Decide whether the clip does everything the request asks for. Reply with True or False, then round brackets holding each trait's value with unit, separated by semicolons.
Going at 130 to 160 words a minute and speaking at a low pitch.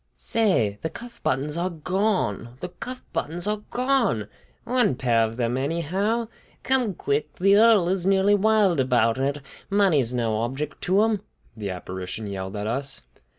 False (155 wpm; 160 Hz)